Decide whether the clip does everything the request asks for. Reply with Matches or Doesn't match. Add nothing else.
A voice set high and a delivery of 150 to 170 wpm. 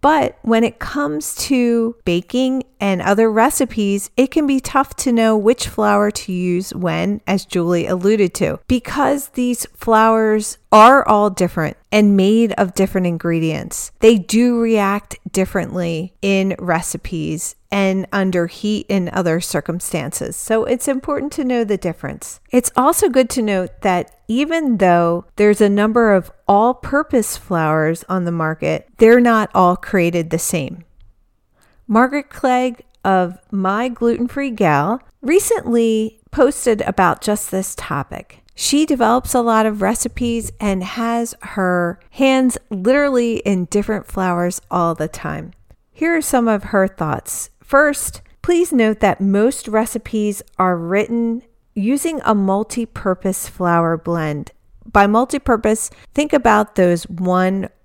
Doesn't match